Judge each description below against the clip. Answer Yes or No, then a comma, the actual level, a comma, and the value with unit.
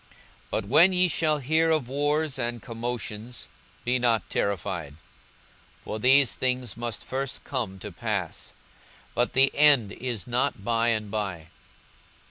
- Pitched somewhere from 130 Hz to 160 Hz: No, low, 120 Hz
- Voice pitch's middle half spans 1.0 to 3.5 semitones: No, average, 4.4 semitones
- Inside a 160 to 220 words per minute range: No, average, 140 wpm